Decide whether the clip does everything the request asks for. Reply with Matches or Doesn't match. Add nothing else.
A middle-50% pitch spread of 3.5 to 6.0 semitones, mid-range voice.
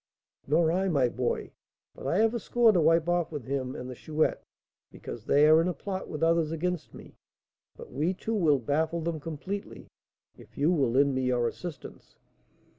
Matches